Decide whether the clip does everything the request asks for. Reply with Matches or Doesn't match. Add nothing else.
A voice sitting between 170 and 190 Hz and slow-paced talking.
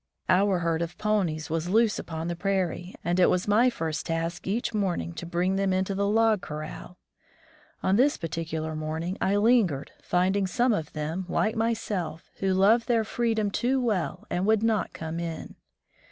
Doesn't match